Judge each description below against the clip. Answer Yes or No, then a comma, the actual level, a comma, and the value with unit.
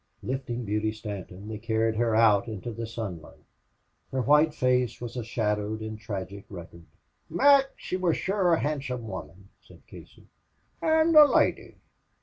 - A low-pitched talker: Yes, low, 115 Hz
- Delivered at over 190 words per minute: No, average, 150 wpm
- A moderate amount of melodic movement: Yes, average, 4.3 semitones